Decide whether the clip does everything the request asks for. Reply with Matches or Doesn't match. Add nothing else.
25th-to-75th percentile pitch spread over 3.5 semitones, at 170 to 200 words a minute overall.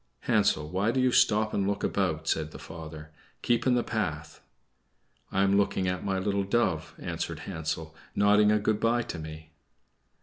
Matches